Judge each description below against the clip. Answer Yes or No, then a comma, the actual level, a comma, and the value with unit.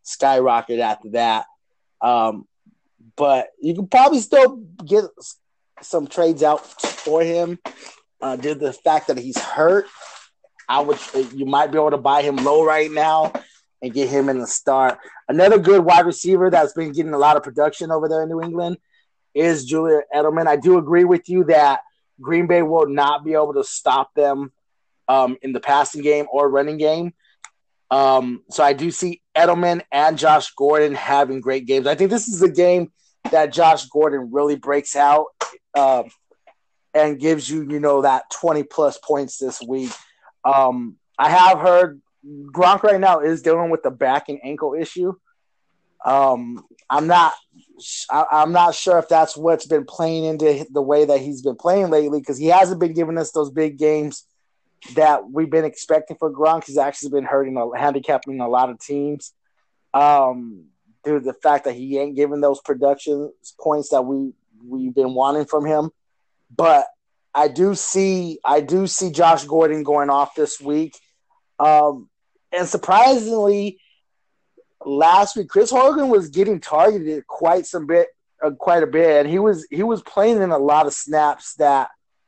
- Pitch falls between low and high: Yes, medium, 155 Hz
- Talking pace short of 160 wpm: No, average, 175 wpm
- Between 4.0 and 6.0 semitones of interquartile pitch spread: No, average, 3.6 semitones